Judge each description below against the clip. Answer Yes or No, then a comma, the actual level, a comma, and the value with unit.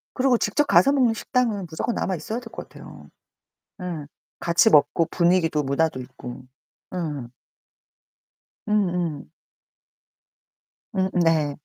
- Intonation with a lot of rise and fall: Yes, wide, 6.1 semitones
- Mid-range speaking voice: Yes, medium, 175 Hz